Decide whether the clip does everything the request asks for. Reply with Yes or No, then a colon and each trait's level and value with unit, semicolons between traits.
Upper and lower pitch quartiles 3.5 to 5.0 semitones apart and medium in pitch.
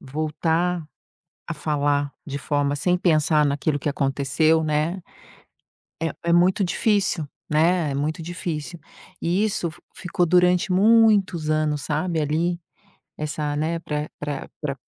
No: average, 2.9 semitones; medium, 155 Hz